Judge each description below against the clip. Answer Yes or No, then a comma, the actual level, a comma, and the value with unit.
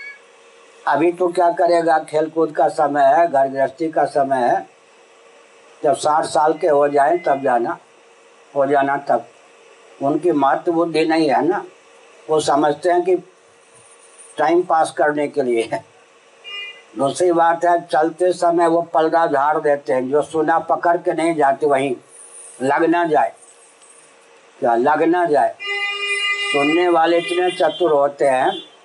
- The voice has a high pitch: No, medium, 170 Hz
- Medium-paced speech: Yes, average, 145 wpm